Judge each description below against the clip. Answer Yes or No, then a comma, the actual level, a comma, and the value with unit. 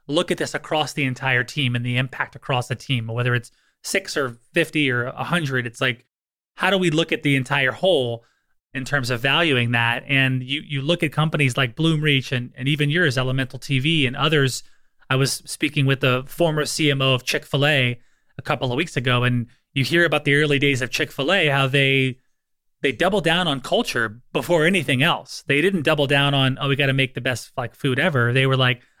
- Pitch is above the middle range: No, low, 135 Hz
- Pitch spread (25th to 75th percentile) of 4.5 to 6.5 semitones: No, average, 3.0 semitones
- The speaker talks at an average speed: No, fast, 215 wpm